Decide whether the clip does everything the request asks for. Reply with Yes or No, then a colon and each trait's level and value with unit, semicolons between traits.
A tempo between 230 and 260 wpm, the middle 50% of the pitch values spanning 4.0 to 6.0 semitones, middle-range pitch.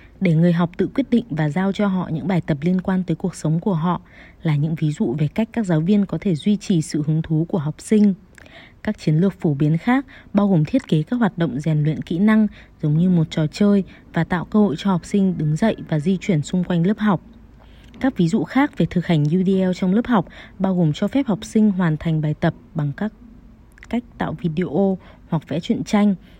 Yes: average, 245 wpm; average, 4.3 semitones; medium, 180 Hz